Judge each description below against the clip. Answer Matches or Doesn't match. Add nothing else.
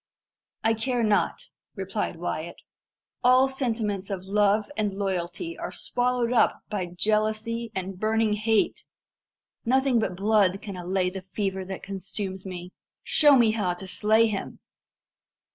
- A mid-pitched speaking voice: Doesn't match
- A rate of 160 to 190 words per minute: Doesn't match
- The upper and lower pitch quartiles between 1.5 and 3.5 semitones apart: Matches